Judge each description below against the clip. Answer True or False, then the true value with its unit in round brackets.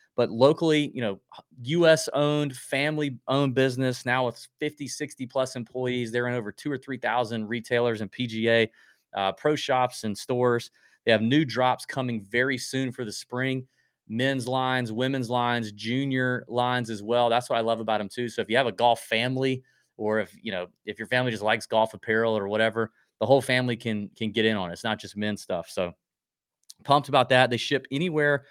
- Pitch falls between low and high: False (125 Hz)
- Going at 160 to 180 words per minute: False (200 wpm)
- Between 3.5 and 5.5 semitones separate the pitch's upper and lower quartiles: False (2.8 semitones)